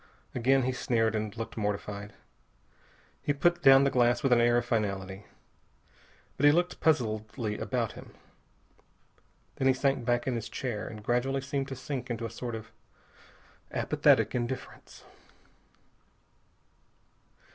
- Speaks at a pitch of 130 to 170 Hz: No, low, 120 Hz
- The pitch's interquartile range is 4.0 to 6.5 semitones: No, average, 3.4 semitones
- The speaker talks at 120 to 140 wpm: Yes, slow, 135 wpm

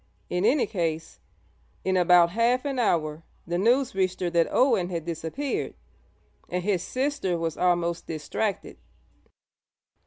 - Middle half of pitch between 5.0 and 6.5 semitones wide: Yes, average, 5.3 semitones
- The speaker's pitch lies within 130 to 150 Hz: No, medium, 180 Hz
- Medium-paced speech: No, slow, 130 wpm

